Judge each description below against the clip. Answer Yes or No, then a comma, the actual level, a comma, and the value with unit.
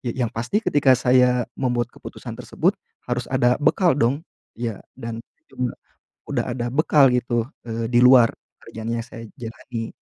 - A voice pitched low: Yes, low, 120 Hz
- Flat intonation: Yes, narrow, 1.9 semitones